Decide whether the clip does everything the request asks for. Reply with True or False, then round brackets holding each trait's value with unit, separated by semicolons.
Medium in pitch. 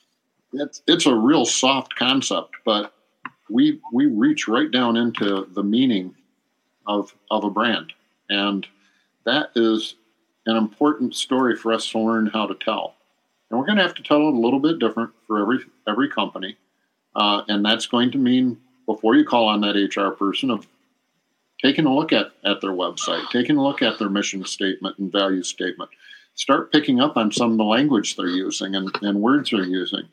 False (110 Hz)